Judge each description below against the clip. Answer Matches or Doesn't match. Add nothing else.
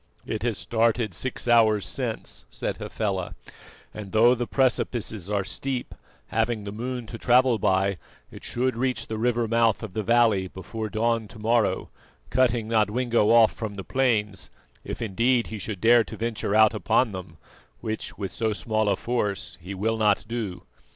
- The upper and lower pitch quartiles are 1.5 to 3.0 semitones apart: Matches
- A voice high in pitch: Doesn't match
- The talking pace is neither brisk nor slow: Matches